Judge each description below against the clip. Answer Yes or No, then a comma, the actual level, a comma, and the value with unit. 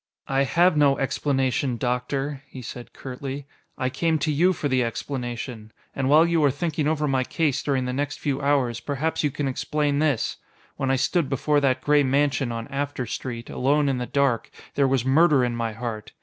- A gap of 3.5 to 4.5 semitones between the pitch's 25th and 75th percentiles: No, narrow, 2.5 semitones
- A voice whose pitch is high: No, low, 135 Hz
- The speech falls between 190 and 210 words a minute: Yes, average, 195 wpm